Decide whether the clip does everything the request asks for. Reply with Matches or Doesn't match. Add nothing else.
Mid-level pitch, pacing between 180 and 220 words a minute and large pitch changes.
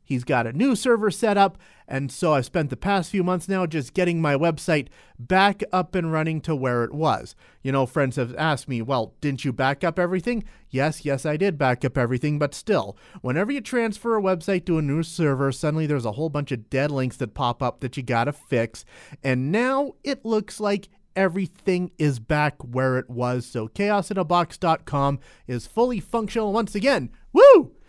Matches